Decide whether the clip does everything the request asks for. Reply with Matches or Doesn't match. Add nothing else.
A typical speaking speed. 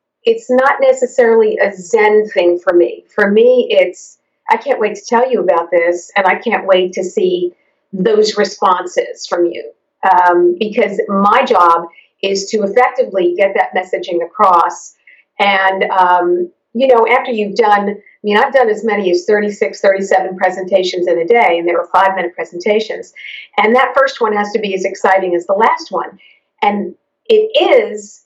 Matches